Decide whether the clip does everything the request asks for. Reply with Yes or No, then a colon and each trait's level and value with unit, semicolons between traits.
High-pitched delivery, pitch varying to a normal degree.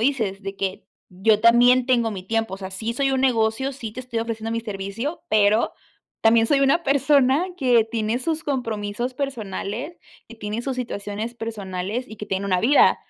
Yes: high, 230 Hz; average, 3.6 semitones